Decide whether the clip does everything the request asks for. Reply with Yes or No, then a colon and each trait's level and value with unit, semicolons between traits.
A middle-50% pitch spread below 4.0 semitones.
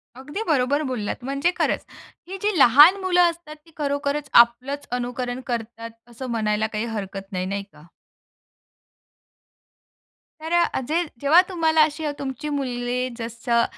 No: average, 4.7 semitones